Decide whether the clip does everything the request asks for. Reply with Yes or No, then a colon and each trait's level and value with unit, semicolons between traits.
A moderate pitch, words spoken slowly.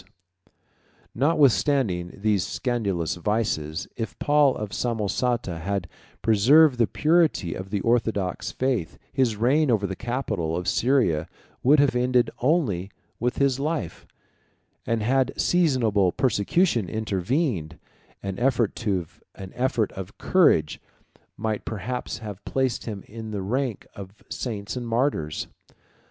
No: low, 115 Hz; slow, 120 wpm